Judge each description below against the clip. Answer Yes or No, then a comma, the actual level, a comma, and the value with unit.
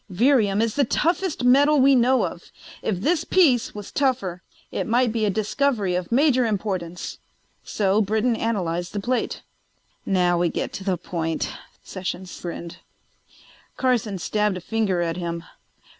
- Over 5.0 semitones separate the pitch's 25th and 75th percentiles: Yes, wide, 5.6 semitones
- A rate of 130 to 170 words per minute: Yes, average, 150 wpm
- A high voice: Yes, high, 210 Hz